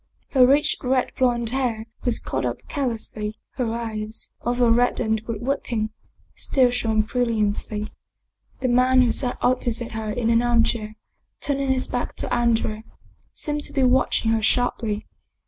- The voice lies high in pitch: Yes, high, 240 Hz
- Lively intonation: No, narrow, 2.4 semitones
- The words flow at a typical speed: Yes, average, 145 wpm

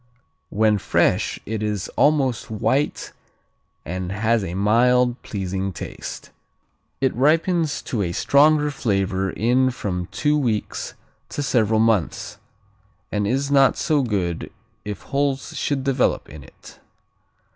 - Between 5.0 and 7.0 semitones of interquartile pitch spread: Yes, wide, 5.5 semitones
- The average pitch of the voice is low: Yes, low, 115 Hz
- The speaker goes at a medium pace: No, slow, 125 wpm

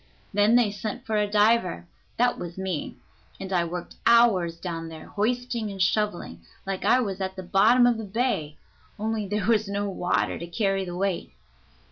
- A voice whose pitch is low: No, high, 200 Hz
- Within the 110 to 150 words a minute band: No, average, 180 wpm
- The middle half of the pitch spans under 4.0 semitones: Yes, average, 3.5 semitones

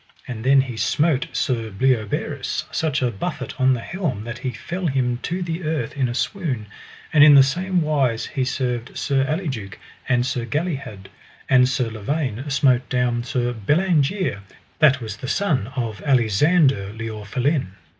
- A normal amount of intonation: Yes, average, 4.2 semitones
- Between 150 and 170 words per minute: Yes, average, 165 wpm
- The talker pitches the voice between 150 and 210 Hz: No, low, 130 Hz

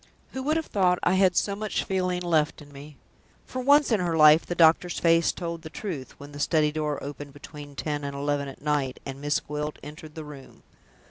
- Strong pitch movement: No, average, 3.6 semitones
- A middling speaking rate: No, fast, 215 wpm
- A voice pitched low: No, medium, 155 Hz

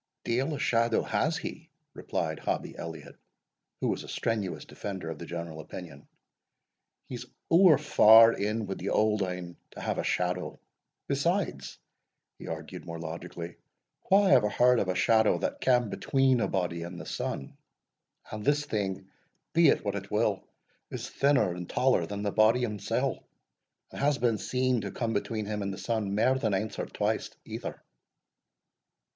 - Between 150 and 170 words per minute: Yes, average, 165 wpm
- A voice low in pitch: Yes, low, 110 Hz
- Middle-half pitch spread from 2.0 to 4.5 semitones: No, wide, 5.5 semitones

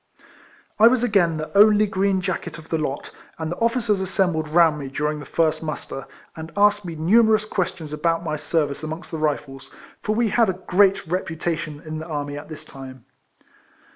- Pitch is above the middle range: No, medium, 165 Hz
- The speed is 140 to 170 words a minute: No, average, 185 wpm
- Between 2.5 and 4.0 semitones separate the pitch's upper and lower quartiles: No, average, 4.4 semitones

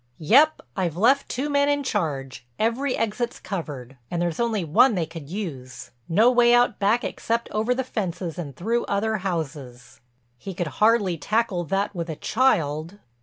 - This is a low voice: No, high, 195 Hz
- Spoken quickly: No, average, 155 wpm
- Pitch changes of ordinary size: No, wide, 6.6 semitones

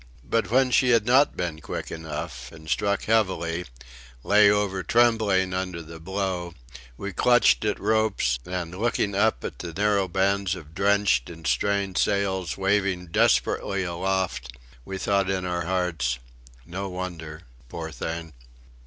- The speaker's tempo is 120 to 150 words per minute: Yes, average, 145 wpm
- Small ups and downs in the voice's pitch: No, average, 3.2 semitones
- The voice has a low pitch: Yes, very low, 95 Hz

